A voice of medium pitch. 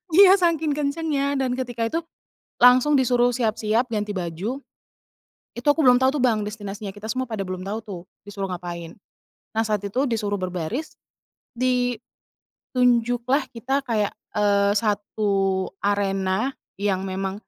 No: high, 220 Hz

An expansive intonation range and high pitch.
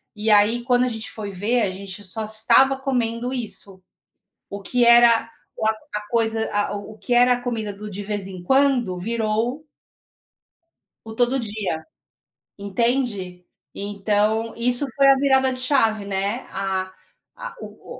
No: average, 3.3 semitones; high, 220 Hz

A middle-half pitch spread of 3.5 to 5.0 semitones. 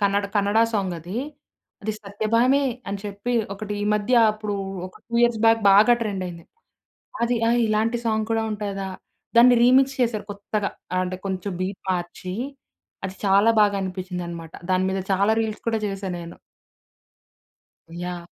No: average, 3.0 semitones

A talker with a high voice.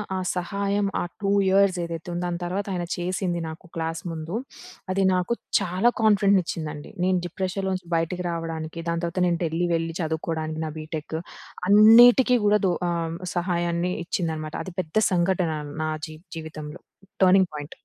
No: medium, 175 Hz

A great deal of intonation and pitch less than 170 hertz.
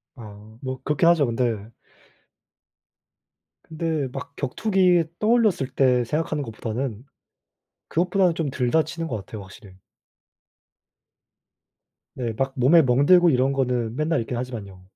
Yes: wide, 5.7 semitones; low, 135 Hz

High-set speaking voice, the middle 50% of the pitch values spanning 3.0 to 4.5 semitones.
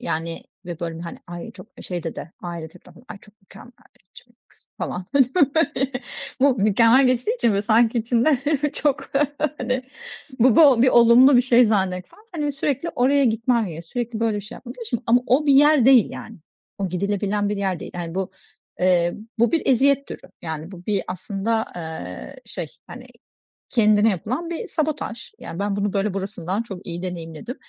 No: high, 220 Hz; wide, 5.5 semitones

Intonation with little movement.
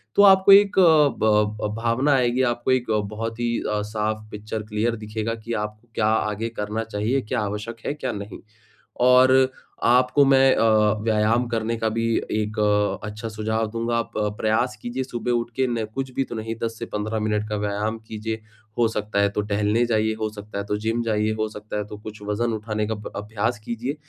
Yes: narrow, 2.0 semitones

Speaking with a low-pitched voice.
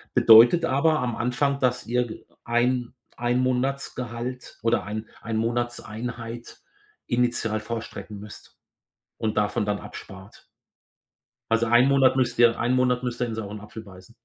Yes: low, 120 Hz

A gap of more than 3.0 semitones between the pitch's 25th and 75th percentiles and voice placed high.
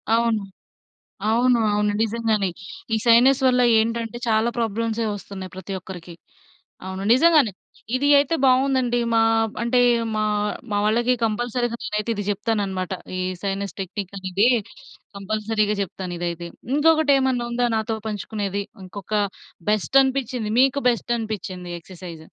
Yes: average, 3.4 semitones; high, 220 Hz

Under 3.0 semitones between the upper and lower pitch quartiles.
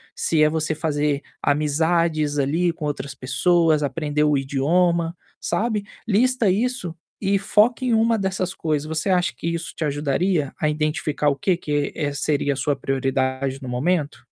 No: average, 3.8 semitones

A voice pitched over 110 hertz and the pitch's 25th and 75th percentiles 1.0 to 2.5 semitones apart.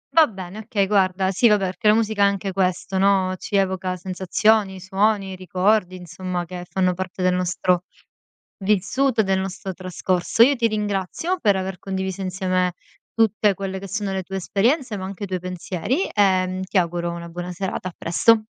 Yes: high, 190 Hz; narrow, 2.0 semitones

